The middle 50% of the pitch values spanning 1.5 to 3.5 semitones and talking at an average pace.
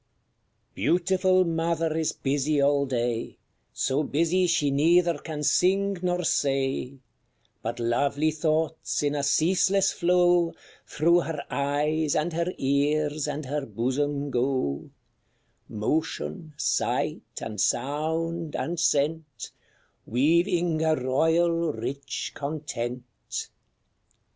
No: average, 3.2 semitones; slow, 105 wpm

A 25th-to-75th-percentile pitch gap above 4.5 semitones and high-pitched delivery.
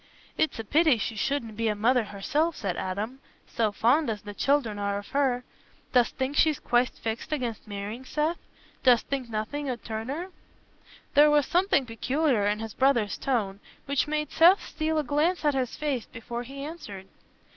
Yes: average, 5.1 semitones; very high, 255 Hz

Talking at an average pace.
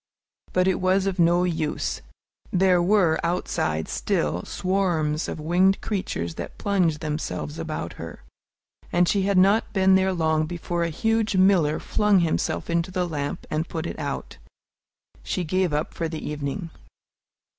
Yes: average, 155 wpm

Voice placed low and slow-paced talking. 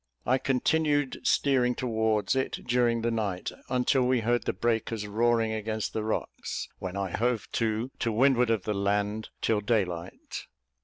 No: low, 115 Hz; average, 155 wpm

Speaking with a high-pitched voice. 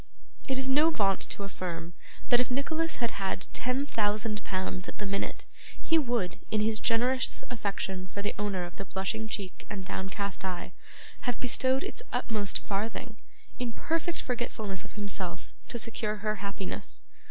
Yes: high, 210 Hz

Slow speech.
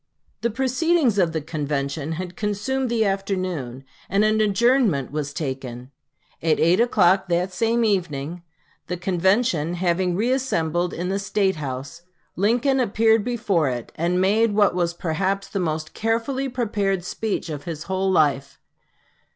No: average, 145 wpm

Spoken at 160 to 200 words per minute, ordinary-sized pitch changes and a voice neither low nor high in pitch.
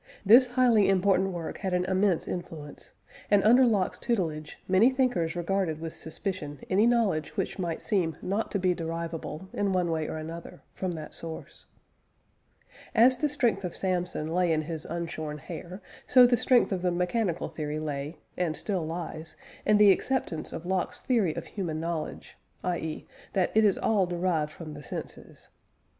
Yes: average, 170 wpm; average, 3.9 semitones; medium, 180 Hz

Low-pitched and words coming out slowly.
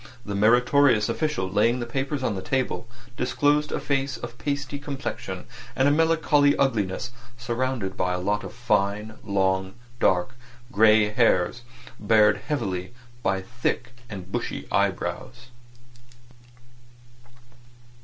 Yes: low, 120 Hz; slow, 120 wpm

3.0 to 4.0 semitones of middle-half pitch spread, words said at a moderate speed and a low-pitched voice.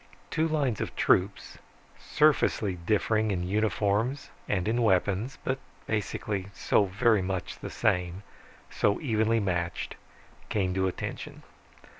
No: average, 3.4 semitones; slow, 115 wpm; low, 105 Hz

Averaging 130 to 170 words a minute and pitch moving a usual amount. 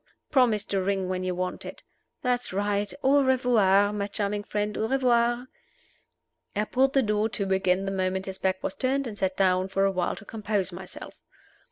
No: average, 190 wpm; average, 3.8 semitones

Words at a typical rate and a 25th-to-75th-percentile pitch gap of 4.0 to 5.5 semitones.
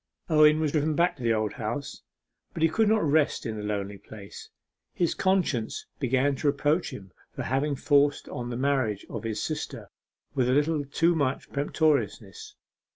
Yes: average, 175 wpm; average, 4.8 semitones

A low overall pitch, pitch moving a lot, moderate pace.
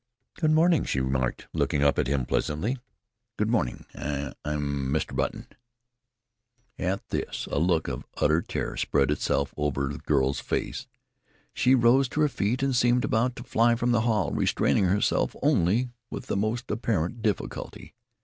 Yes: low, 100 Hz; wide, 8.8 semitones; average, 165 wpm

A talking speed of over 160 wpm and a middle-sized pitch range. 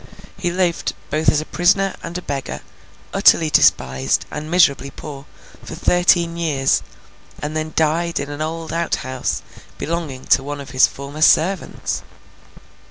No: average, 145 wpm; average, 3.3 semitones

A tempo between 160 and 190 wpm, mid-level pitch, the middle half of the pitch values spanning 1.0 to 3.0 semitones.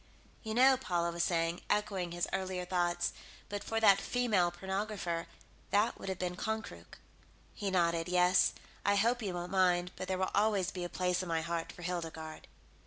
Yes: average, 180 wpm; medium, 180 Hz; narrow, 2.6 semitones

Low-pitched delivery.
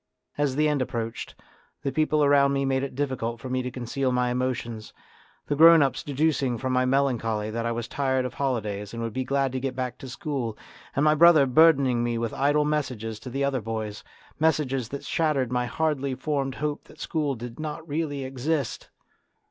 Yes: low, 130 Hz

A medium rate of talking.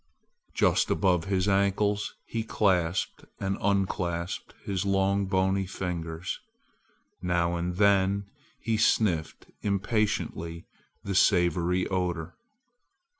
No: slow, 95 wpm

